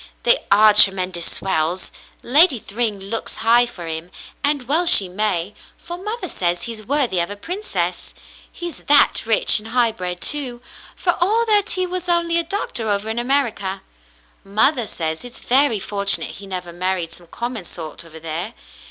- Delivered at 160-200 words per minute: Yes, average, 170 wpm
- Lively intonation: Yes, wide, 7.6 semitones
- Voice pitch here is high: Yes, high, 220 Hz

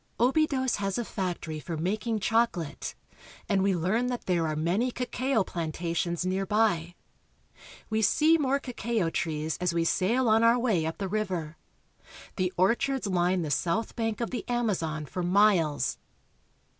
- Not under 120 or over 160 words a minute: Yes, average, 155 wpm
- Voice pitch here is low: No, high, 195 Hz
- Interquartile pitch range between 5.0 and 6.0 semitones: Yes, average, 5.3 semitones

